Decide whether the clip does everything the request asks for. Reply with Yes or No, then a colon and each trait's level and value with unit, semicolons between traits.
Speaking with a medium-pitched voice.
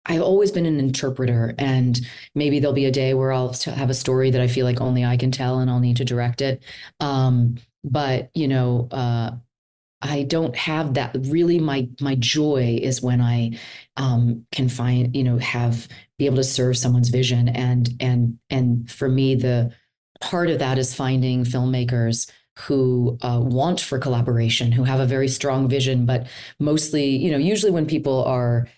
No: low, 130 Hz